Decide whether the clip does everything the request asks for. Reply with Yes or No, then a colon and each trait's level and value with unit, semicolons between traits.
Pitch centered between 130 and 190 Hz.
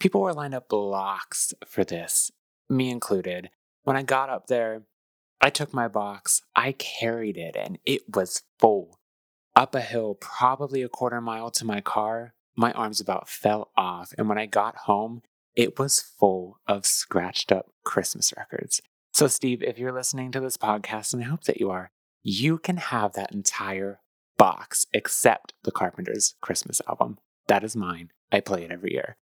No: low, 115 Hz